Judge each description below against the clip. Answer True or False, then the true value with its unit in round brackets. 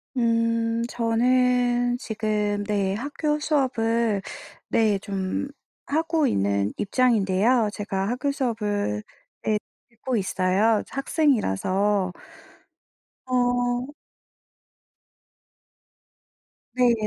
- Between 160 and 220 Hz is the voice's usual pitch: False (230 Hz)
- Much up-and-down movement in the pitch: False (3.5 semitones)